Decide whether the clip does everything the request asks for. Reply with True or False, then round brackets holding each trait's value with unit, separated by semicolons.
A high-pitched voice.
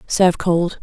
False (175 Hz)